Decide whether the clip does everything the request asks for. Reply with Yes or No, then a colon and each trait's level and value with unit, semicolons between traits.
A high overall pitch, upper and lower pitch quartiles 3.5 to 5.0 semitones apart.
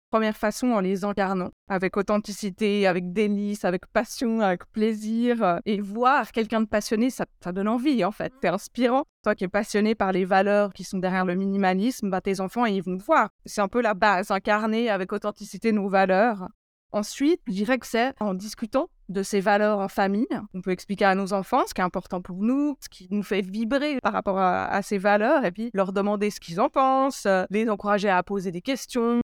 No: high, 205 Hz; average, 2.7 semitones